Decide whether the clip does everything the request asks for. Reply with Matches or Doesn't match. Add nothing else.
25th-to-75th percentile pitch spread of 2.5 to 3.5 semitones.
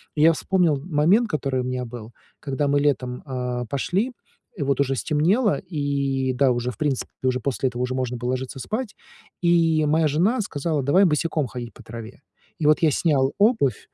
Doesn't match